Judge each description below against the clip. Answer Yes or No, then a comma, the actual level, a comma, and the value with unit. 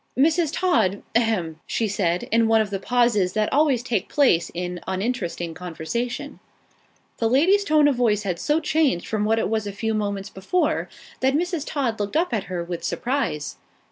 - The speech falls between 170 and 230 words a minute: Yes, average, 185 wpm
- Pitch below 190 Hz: No, high, 225 Hz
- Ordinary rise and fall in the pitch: No, wide, 6.5 semitones